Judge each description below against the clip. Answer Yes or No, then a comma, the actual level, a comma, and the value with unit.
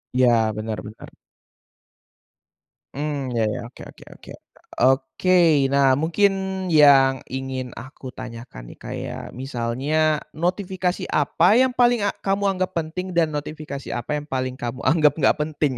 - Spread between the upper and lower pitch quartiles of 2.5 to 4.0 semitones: No, average, 4.9 semitones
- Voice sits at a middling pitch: Yes, medium, 145 Hz